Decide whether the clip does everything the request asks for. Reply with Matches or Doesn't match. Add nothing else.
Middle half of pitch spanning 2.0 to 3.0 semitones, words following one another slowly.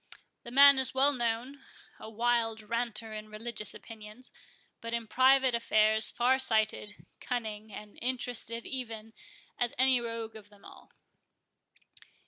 Matches